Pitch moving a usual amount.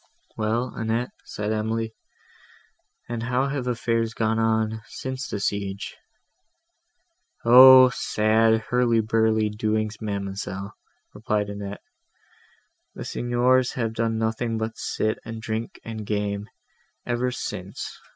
No: narrow, 1.9 semitones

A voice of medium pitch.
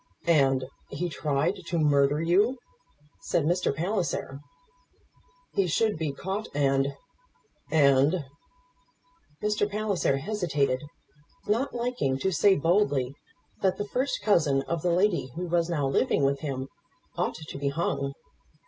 Yes: medium, 165 Hz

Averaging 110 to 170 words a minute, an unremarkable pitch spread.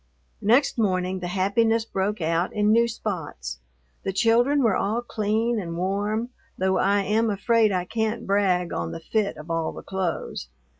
Yes: average, 165 wpm; average, 3.5 semitones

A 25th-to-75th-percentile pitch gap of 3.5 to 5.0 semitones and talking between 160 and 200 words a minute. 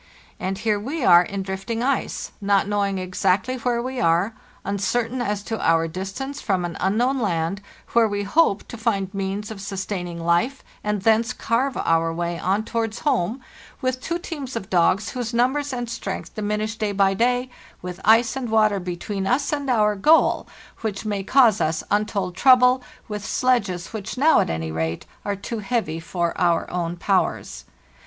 Yes: average, 4.4 semitones; average, 175 wpm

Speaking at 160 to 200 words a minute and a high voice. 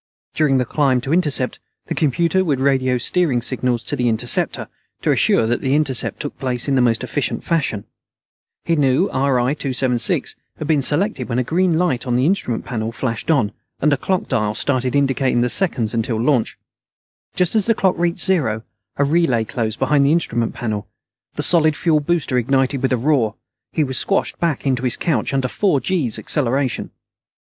No: average, 185 wpm; low, 135 Hz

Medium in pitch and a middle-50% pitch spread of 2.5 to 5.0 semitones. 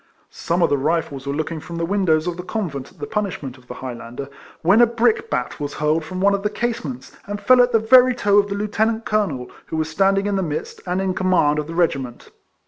No: medium, 180 Hz; wide, 5.6 semitones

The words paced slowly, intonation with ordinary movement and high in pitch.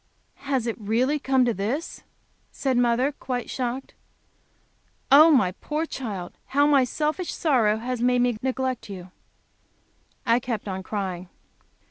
Yes: slow, 130 wpm; average, 3.8 semitones; very high, 250 Hz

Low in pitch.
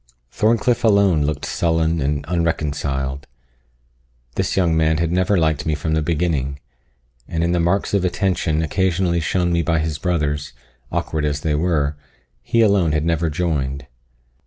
Yes: very low, 80 Hz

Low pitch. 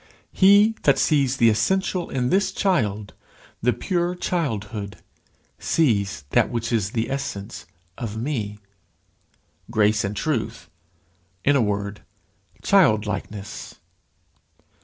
Yes: low, 115 Hz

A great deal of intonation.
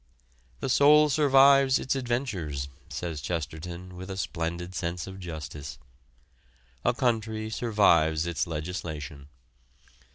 Yes: wide, 7.1 semitones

